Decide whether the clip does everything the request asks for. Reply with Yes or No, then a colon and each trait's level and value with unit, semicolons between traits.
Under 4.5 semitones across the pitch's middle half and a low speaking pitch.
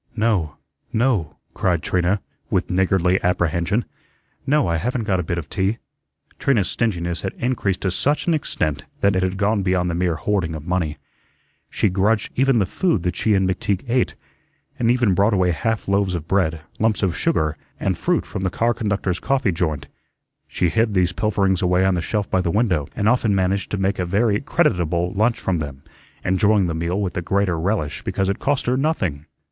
Yes: average, 3.6 semitones; very low, 95 Hz